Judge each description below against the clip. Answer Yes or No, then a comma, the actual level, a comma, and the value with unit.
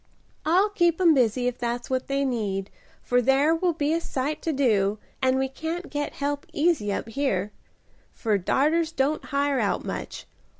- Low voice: No, very high, 275 Hz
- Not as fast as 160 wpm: No, average, 175 wpm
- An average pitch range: Yes, average, 4.5 semitones